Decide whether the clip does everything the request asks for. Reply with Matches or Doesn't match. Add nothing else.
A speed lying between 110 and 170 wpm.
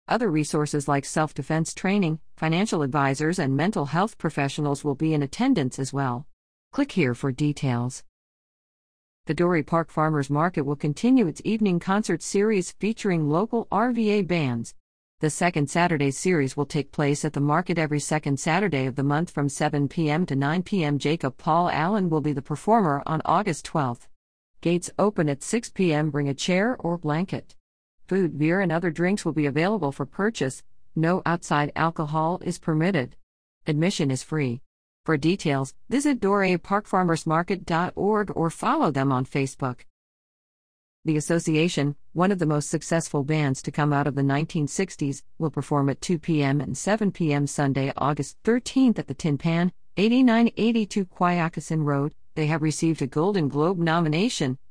Matches